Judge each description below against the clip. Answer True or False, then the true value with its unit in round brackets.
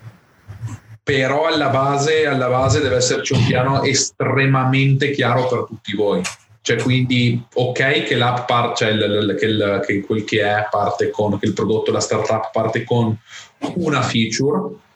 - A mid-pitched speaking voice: False (125 Hz)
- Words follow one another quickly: False (150 wpm)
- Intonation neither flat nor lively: True (3.4 semitones)